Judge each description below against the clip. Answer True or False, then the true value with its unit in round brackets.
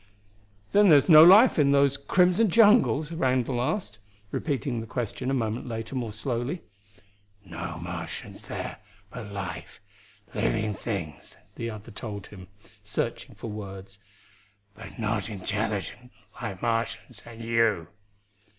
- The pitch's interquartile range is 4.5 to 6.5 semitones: True (5.1 semitones)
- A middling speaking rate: False (125 wpm)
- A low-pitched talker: True (115 Hz)